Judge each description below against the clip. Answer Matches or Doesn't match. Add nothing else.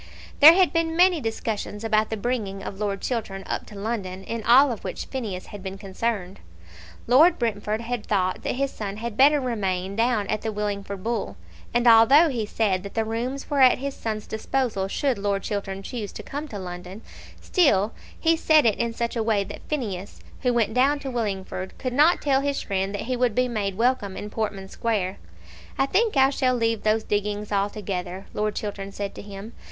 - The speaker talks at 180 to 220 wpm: Matches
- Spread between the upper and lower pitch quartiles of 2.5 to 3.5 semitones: Doesn't match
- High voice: Matches